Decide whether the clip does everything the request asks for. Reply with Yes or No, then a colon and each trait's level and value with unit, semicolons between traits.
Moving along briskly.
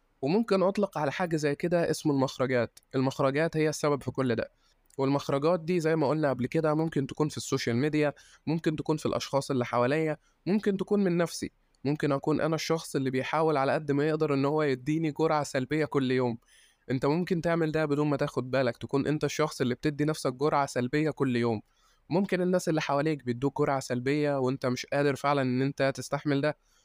Yes: fast, 190 wpm